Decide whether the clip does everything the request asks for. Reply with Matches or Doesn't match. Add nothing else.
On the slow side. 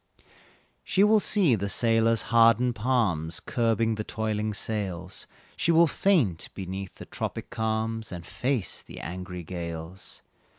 Matches